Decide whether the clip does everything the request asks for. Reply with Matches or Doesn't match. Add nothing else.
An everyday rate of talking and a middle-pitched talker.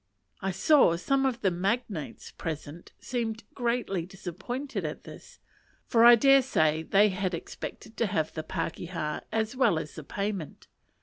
Doesn't match